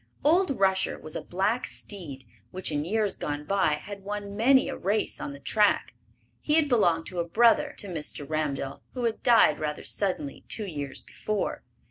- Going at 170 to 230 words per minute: Yes, average, 180 wpm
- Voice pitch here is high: Yes, high, 195 Hz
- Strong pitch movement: Yes, wide, 6.2 semitones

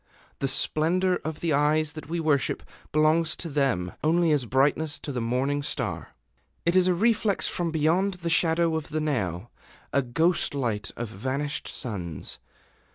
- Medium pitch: Yes, medium, 155 Hz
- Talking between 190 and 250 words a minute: No, average, 160 wpm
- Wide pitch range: No, average, 4.0 semitones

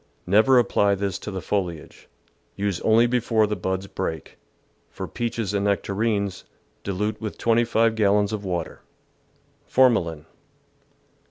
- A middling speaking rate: No, slow, 125 wpm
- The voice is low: Yes, low, 105 Hz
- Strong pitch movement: No, average, 2.8 semitones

